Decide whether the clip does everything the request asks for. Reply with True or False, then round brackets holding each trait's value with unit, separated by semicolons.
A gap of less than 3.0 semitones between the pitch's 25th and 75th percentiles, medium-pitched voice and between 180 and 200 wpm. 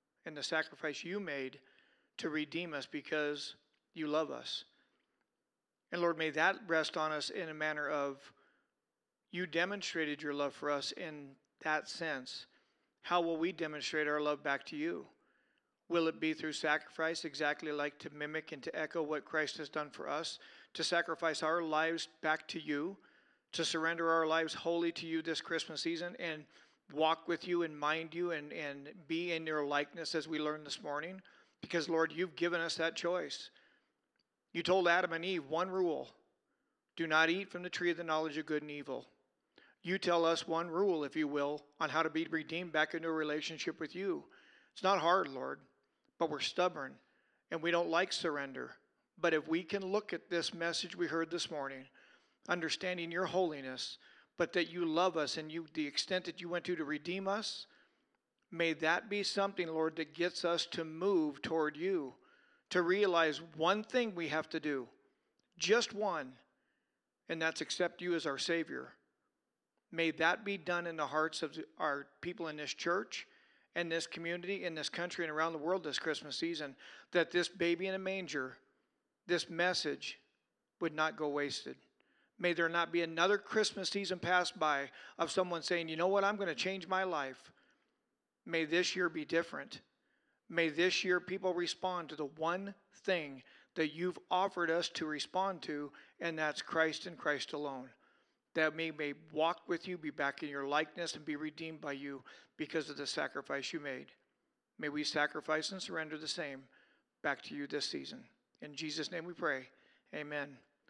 True (2.4 semitones; 165 Hz; 185 wpm)